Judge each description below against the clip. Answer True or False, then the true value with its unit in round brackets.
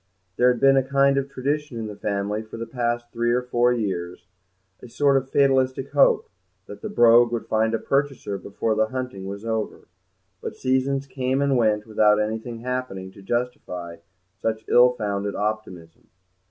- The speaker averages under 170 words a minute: False (175 wpm)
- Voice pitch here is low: True (120 Hz)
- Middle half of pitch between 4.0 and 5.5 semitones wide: False (3.6 semitones)